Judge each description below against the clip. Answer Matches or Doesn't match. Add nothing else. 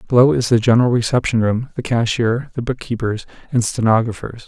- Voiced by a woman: Doesn't match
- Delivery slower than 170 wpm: Matches